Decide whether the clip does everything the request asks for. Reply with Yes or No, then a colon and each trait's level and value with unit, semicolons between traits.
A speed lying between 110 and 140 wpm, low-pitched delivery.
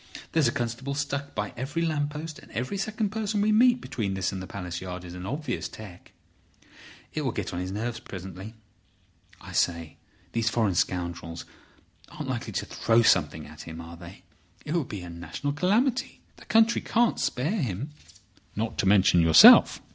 No: average, 175 wpm; low, 115 Hz